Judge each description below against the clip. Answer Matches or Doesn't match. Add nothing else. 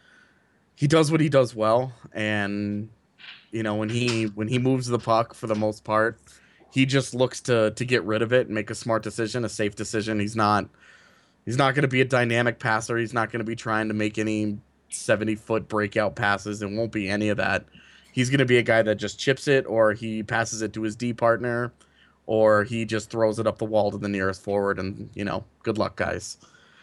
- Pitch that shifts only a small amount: Matches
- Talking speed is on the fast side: Matches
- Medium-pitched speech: Doesn't match